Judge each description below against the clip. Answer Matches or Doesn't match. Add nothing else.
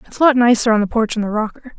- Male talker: Doesn't match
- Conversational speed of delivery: Doesn't match